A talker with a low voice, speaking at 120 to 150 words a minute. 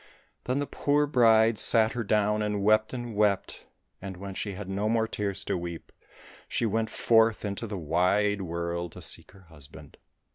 No: low, 105 Hz; average, 180 wpm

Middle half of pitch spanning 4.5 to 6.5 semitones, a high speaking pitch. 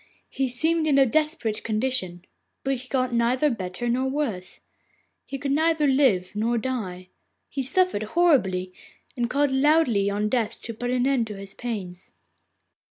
Yes: average, 4.8 semitones; high, 245 Hz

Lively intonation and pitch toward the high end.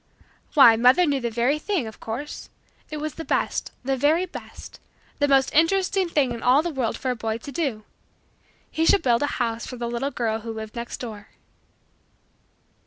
No: average, 4.5 semitones; very high, 260 Hz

